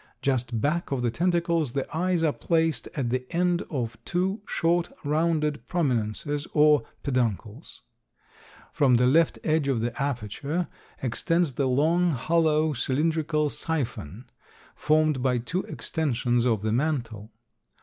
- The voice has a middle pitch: Yes, medium, 145 Hz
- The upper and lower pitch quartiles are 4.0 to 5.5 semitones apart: Yes, average, 4.8 semitones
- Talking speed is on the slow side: Yes, slow, 130 wpm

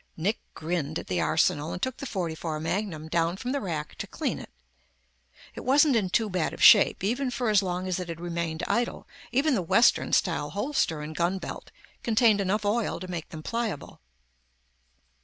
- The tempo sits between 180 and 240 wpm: Yes, average, 185 wpm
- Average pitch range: No, wide, 5.7 semitones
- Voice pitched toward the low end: No, medium, 185 Hz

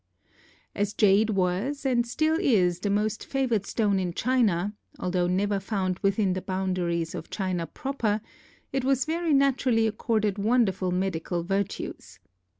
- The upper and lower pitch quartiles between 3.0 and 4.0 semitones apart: No, average, 4.4 semitones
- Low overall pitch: No, high, 205 Hz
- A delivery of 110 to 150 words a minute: Yes, average, 140 wpm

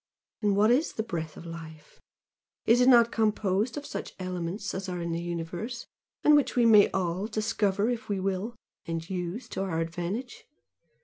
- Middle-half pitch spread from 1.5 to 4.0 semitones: No, average, 4.8 semitones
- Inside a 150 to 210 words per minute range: Yes, average, 180 wpm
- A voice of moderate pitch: No, high, 195 Hz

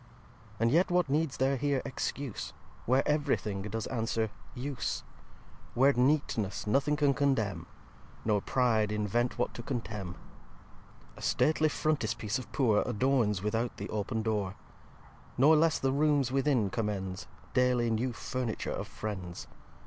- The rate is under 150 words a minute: Yes, average, 140 wpm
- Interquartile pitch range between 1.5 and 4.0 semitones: No, average, 4.6 semitones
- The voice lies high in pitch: No, low, 120 Hz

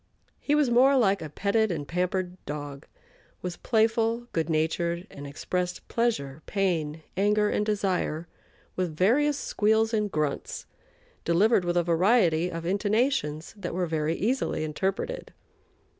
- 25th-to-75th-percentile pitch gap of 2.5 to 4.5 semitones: No, average, 5.2 semitones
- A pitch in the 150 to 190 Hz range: Yes, medium, 185 Hz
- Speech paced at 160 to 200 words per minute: No, slow, 135 wpm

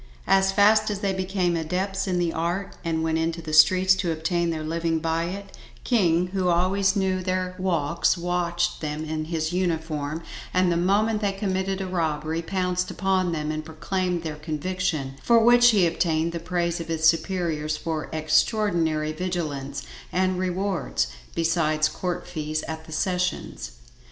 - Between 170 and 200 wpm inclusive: No, average, 160 wpm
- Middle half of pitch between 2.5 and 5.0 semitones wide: Yes, average, 2.8 semitones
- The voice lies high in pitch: No, medium, 175 Hz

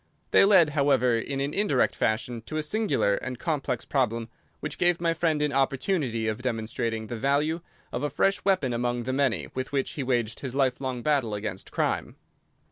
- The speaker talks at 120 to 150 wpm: No, average, 190 wpm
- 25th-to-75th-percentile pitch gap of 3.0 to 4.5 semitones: Yes, average, 4.1 semitones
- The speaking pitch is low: Yes, low, 130 Hz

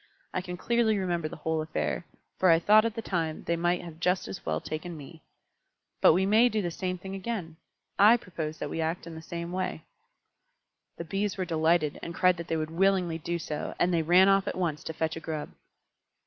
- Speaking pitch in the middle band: Yes, medium, 170 Hz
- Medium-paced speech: No, fast, 225 wpm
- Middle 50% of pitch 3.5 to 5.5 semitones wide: No, average, 2.8 semitones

